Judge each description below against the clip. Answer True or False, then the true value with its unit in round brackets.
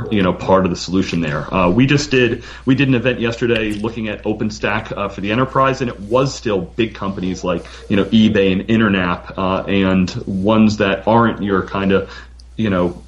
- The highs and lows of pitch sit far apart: False (3.6 semitones)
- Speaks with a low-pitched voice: True (105 Hz)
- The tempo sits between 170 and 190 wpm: False (205 wpm)